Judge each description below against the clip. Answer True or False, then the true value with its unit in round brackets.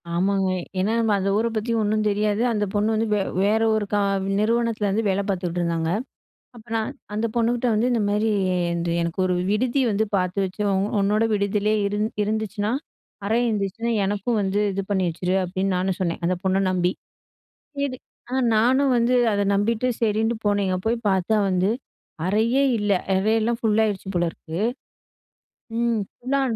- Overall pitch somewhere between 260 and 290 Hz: False (210 Hz)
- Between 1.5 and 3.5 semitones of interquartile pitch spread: True (2.7 semitones)